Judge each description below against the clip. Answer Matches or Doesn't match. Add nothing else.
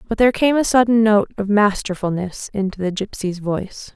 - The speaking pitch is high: Matches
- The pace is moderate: Matches